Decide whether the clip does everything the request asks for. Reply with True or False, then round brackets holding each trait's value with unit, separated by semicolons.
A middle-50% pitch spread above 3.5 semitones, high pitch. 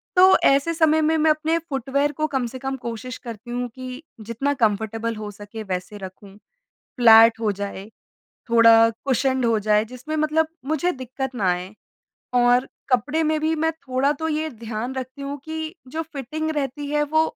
True (5.2 semitones; 260 Hz)